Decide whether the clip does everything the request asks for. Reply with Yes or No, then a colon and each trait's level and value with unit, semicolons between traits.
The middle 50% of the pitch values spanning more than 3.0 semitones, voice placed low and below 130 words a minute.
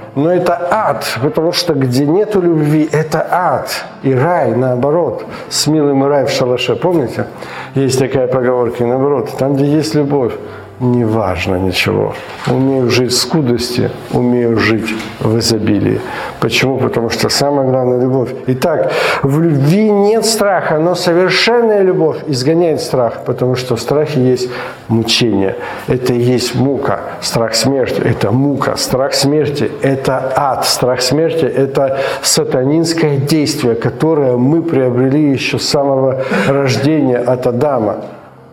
No: average, 3.6 semitones; low, 130 Hz; average, 135 wpm